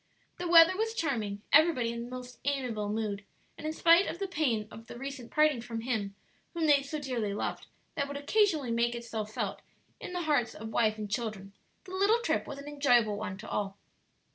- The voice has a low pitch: No, very high, 250 Hz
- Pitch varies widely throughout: Yes, wide, 5.9 semitones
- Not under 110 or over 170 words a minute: No, average, 195 wpm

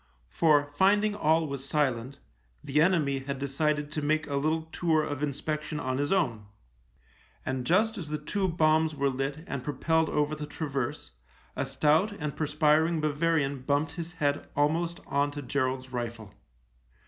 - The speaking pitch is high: No, medium, 150 Hz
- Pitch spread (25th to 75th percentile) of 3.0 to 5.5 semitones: No, narrow, 2.4 semitones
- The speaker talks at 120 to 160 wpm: No, average, 170 wpm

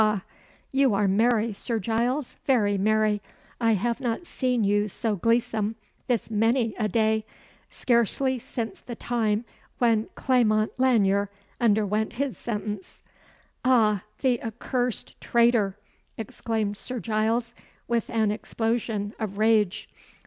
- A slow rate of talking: Yes, slow, 120 wpm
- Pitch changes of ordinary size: No, narrow, 2.2 semitones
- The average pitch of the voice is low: No, high, 225 Hz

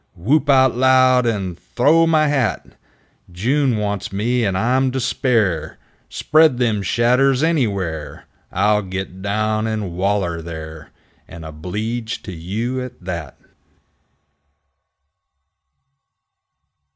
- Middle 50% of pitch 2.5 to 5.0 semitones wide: No, wide, 5.5 semitones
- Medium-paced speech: No, slow, 105 wpm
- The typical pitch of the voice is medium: No, low, 110 Hz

